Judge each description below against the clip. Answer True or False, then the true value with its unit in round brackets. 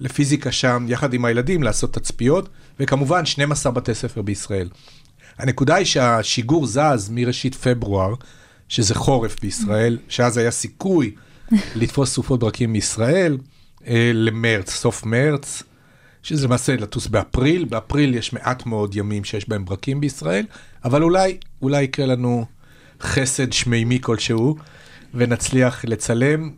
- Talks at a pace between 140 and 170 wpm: False (120 wpm)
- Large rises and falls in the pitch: False (3.4 semitones)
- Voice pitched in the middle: False (125 Hz)